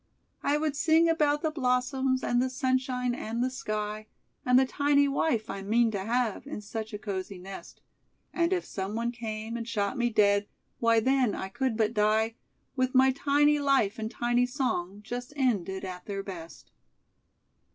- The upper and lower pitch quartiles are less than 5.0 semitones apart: Yes, average, 3.9 semitones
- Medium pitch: No, high, 240 Hz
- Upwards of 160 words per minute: Yes, average, 170 wpm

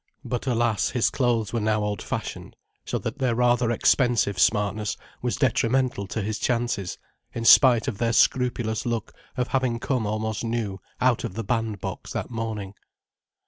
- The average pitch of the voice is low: Yes, low, 115 Hz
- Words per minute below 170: Yes, average, 160 wpm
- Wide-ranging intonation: No, narrow, 2.4 semitones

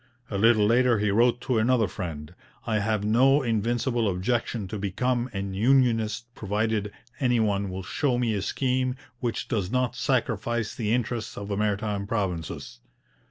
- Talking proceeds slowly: No, average, 160 wpm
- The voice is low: Yes, low, 110 Hz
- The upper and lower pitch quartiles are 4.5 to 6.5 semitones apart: No, average, 3.2 semitones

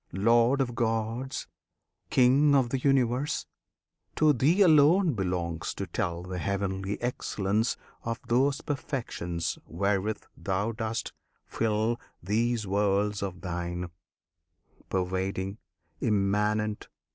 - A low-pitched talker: Yes, low, 110 Hz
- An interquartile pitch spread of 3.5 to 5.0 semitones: Yes, average, 4.4 semitones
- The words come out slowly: Yes, slow, 100 wpm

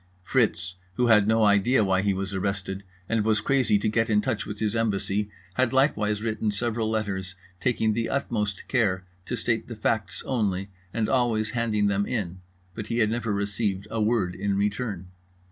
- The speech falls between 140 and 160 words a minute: No, average, 180 wpm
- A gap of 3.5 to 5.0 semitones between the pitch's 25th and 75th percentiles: No, narrow, 2.4 semitones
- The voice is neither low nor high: No, low, 105 Hz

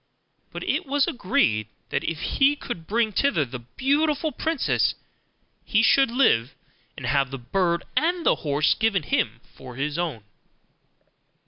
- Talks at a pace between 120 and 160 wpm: Yes, average, 145 wpm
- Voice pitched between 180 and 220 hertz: Yes, medium, 185 Hz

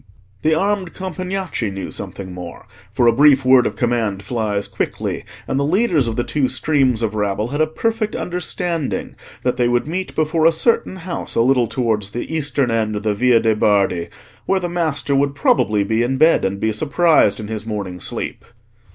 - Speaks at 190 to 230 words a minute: Yes, average, 195 wpm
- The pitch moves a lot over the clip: Yes, wide, 6.7 semitones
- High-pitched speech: No, low, 125 Hz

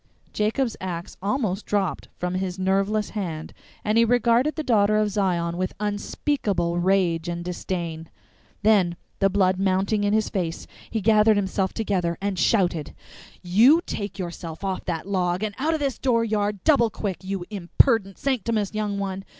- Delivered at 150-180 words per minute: Yes, average, 160 wpm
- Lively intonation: No, average, 3.1 semitones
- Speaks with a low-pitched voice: No, high, 200 Hz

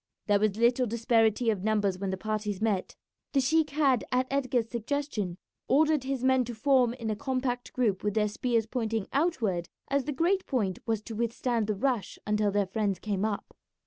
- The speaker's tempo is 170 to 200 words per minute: Yes, average, 190 wpm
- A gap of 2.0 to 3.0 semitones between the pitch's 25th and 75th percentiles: No, average, 3.8 semitones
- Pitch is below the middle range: No, high, 230 Hz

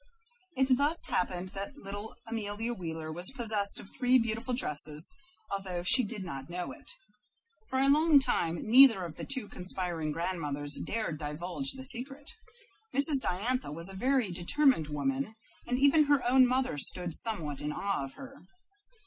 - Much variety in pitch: Yes, wide, 7.2 semitones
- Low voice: No, high, 205 Hz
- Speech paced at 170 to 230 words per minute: No, average, 160 wpm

